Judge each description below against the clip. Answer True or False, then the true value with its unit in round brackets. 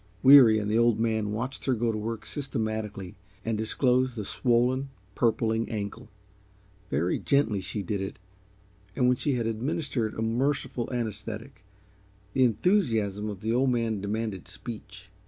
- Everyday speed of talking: True (150 wpm)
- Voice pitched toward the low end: True (115 Hz)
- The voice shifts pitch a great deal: False (2.8 semitones)